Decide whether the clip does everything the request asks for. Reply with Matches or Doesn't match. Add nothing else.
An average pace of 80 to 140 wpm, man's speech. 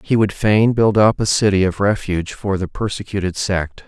Doesn't match